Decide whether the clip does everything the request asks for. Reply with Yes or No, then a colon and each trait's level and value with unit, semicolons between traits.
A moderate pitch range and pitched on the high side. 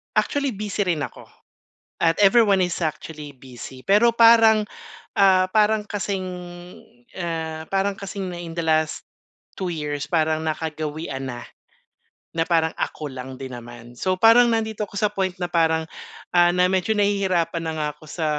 No: average, 4.3 semitones; medium, 175 Hz